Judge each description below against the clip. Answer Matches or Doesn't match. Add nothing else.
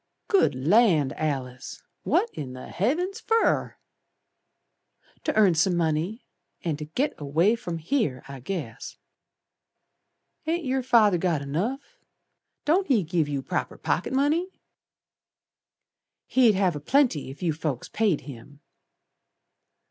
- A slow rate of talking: Matches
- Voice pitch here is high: Doesn't match